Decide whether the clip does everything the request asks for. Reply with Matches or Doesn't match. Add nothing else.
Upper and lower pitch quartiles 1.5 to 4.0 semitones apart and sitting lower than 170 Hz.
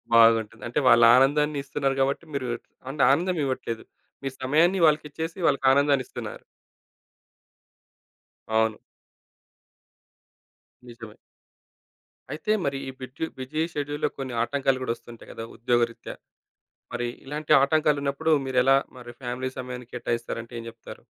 Matches